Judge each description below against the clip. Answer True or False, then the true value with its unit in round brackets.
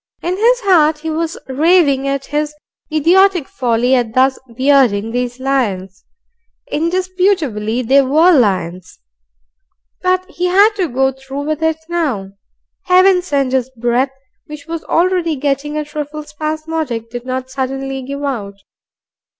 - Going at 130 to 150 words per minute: True (135 wpm)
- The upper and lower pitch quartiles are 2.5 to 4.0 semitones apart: False (4.4 semitones)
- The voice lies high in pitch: True (280 Hz)